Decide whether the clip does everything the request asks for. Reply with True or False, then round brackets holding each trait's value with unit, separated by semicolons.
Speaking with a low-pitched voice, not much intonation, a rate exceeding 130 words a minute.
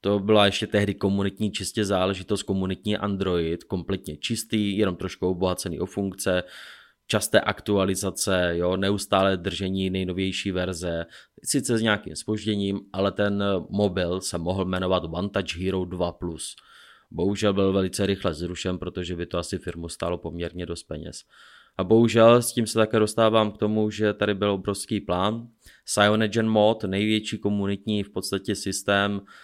True (100 Hz; 2.2 semitones; 145 wpm)